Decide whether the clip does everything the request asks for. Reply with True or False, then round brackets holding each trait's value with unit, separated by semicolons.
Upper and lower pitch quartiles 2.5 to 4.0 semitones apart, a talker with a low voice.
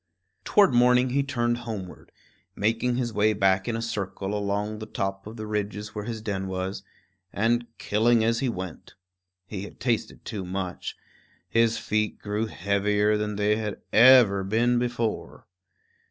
True (2.8 semitones; 110 Hz)